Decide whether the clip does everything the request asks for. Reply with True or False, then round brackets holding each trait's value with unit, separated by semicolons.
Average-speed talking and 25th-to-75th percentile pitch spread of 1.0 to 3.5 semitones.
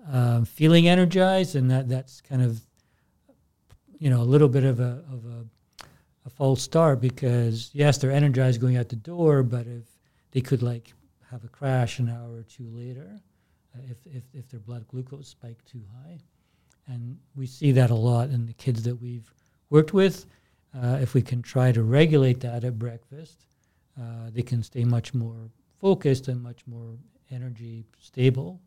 True (180 wpm; 2.5 semitones)